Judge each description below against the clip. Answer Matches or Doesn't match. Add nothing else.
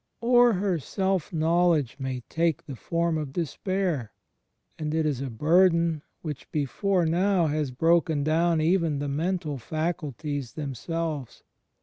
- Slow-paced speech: Matches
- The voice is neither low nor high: Matches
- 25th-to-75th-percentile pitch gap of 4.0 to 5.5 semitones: Doesn't match